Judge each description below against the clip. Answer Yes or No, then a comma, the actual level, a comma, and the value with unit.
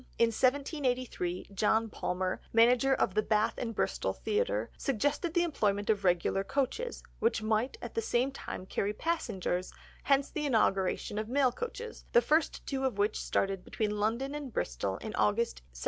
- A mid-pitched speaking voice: No, high, 230 Hz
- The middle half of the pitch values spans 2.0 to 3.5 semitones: No, average, 5.1 semitones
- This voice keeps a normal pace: Yes, average, 165 wpm